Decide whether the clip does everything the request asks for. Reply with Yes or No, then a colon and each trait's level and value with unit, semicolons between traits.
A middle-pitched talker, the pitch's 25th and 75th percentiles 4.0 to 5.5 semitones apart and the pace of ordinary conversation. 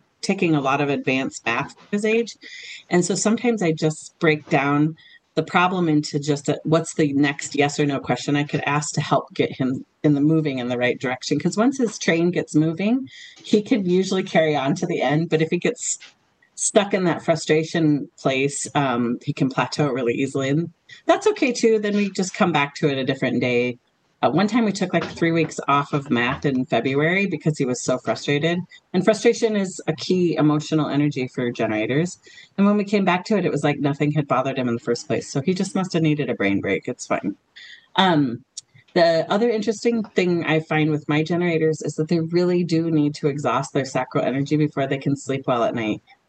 No: medium, 155 Hz; average, 4.6 semitones; fast, 220 wpm